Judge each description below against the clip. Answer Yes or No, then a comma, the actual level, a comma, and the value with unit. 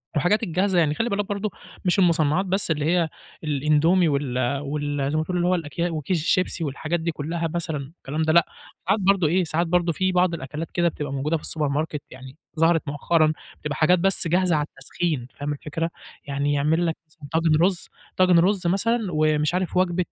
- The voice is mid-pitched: Yes, medium, 165 Hz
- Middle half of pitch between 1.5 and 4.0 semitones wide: Yes, average, 3.2 semitones